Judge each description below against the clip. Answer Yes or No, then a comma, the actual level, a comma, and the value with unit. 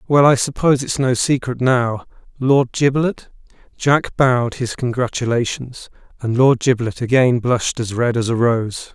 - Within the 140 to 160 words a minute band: Yes, average, 155 wpm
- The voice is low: Yes, low, 125 Hz